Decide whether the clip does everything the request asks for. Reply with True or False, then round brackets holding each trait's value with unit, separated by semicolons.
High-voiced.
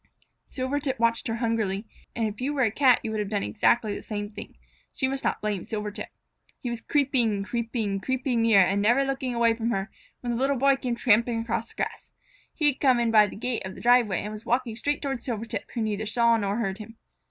True (230 Hz)